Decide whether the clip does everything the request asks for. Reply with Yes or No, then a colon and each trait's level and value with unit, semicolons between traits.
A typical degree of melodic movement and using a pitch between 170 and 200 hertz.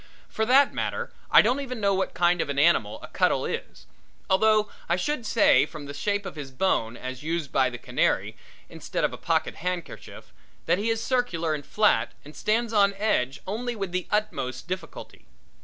No: wide, 6.2 semitones; high, 190 Hz